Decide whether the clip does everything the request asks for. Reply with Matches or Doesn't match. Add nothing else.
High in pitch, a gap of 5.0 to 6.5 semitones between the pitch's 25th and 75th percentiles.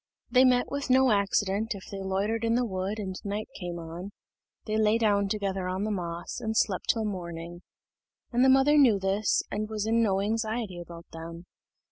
Doesn't match